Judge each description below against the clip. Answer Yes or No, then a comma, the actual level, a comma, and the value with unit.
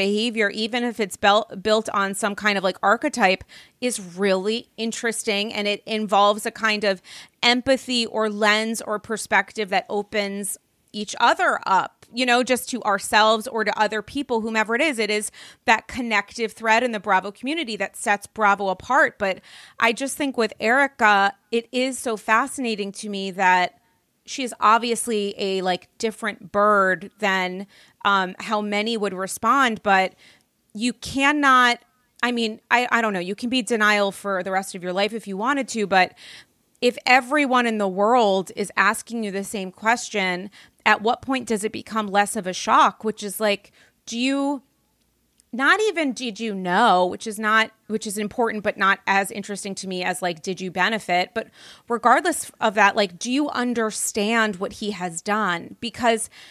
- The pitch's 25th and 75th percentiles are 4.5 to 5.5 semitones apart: No, average, 2.8 semitones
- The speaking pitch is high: Yes, high, 215 Hz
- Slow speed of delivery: No, average, 175 wpm